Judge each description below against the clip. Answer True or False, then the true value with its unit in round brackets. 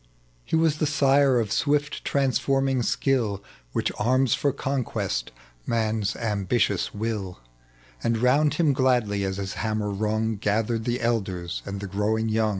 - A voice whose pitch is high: False (115 Hz)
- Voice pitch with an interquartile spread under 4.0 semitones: False (4.5 semitones)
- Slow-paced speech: False (145 wpm)